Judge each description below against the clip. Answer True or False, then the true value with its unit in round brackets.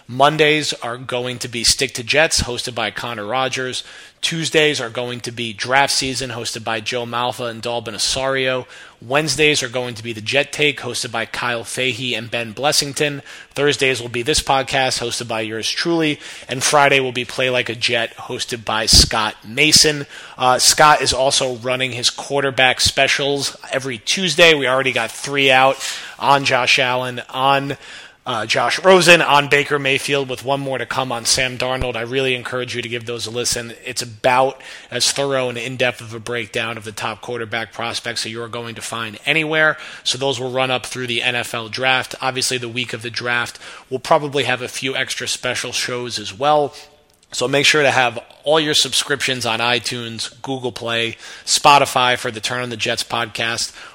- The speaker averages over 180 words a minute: True (190 wpm)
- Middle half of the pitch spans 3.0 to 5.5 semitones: False (2.6 semitones)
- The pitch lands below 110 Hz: False (125 Hz)